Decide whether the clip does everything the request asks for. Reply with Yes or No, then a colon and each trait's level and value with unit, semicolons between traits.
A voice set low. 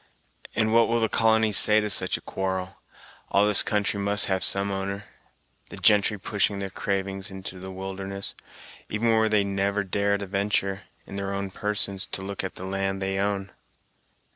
Yes: low, 100 Hz